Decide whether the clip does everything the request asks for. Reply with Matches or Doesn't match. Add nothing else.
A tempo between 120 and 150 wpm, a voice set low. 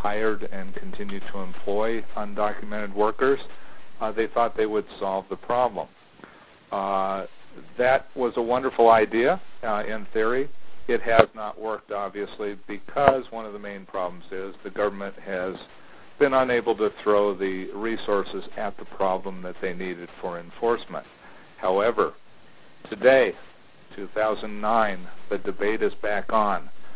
Matches